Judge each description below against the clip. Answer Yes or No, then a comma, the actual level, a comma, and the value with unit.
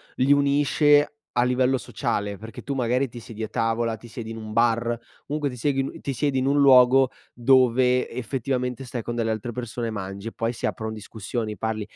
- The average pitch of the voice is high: No, low, 120 Hz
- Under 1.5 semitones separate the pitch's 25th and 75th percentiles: No, average, 2.8 semitones